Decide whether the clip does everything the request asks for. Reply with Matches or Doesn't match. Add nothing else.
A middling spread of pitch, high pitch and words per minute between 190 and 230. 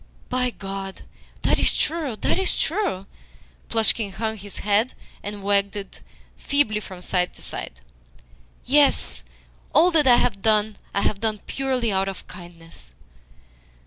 Doesn't match